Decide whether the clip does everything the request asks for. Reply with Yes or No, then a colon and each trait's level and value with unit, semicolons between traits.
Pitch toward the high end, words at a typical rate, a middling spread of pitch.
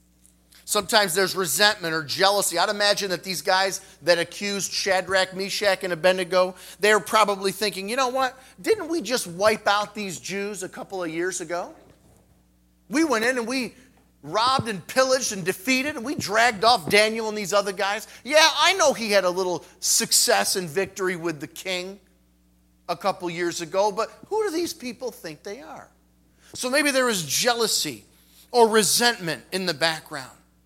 Yes: high, 195 Hz; average, 175 wpm; average, 4.5 semitones